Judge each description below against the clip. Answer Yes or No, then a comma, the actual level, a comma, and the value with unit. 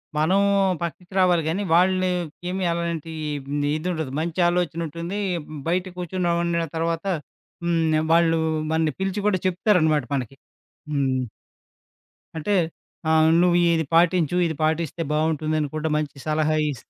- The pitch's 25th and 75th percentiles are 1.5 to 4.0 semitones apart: Yes, narrow, 2.4 semitones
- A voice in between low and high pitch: Yes, medium, 165 Hz